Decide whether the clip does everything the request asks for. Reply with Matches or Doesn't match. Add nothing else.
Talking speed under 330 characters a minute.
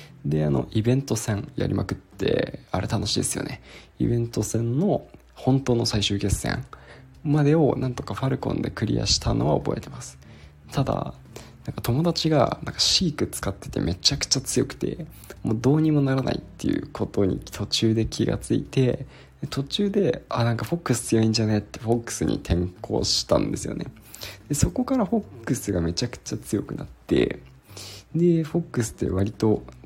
Doesn't match